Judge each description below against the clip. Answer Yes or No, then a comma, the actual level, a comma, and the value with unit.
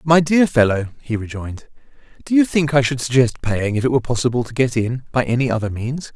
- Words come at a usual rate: No, fast, 225 wpm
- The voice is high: No, low, 125 Hz